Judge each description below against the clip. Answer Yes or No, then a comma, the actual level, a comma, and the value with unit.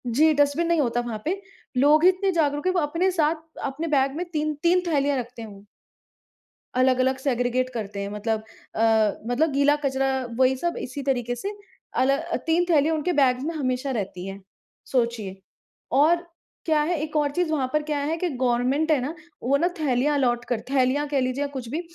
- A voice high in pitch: Yes, very high, 280 Hz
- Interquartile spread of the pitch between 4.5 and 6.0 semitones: No, average, 4.1 semitones